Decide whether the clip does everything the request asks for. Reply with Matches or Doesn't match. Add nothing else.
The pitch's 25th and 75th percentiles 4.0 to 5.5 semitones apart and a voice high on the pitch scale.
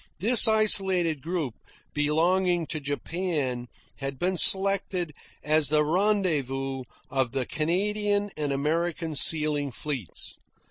Doesn't match